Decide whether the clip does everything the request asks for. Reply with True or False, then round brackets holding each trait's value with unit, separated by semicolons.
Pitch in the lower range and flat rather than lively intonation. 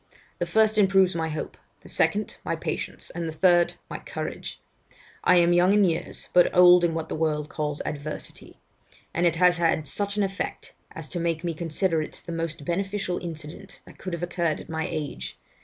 False (170 Hz; 2.1 semitones)